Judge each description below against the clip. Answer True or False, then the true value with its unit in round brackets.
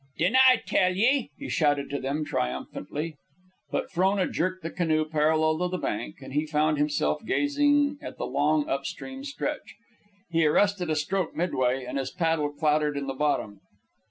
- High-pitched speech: False (155 Hz)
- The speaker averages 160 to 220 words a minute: True (175 wpm)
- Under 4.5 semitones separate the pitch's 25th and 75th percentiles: True (4.1 semitones)